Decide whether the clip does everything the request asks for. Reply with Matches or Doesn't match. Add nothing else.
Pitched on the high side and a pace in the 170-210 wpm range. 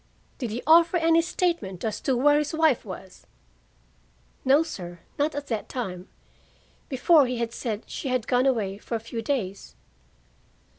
Doesn't match